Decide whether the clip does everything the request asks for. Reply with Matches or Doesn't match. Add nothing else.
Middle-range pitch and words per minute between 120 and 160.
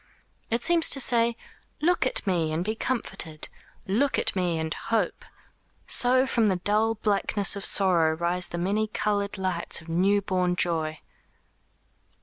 Doesn't match